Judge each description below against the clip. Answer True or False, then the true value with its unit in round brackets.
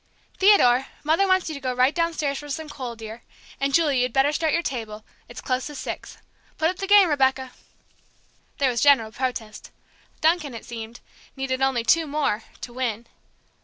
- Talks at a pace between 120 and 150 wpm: False (180 wpm)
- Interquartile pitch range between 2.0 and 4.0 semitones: False (4.4 semitones)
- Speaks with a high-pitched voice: True (270 Hz)